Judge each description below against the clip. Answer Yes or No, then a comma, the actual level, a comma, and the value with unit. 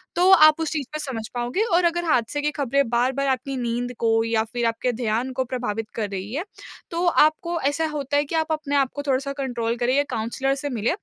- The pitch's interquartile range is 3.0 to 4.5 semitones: Yes, average, 4.1 semitones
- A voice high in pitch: Yes, very high, 265 Hz